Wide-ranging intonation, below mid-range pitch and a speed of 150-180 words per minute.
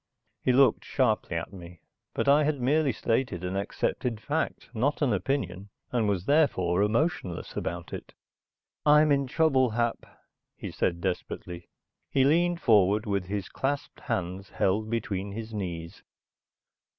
No: wide, 6.6 semitones; low, 110 Hz; average, 140 wpm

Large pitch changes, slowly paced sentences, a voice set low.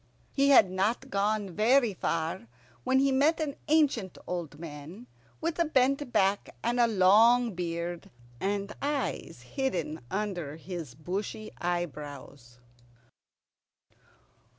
No: wide, 7.2 semitones; slow, 115 wpm; high, 200 Hz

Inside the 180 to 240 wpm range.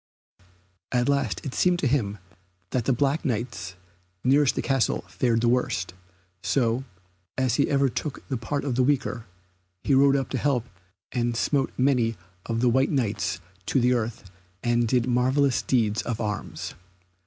No: average, 165 wpm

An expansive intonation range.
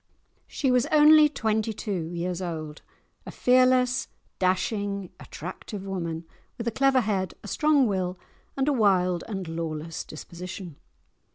Yes: wide, 6.3 semitones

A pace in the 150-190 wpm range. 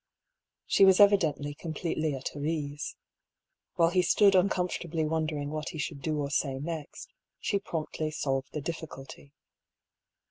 No: average, 140 wpm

